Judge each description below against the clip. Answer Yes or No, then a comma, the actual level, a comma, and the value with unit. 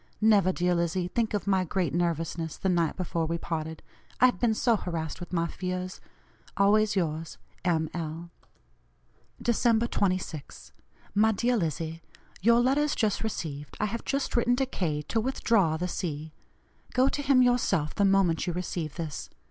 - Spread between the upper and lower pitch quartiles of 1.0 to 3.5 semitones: No, average, 5.1 semitones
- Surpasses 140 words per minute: Yes, average, 165 wpm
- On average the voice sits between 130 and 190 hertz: Yes, medium, 185 Hz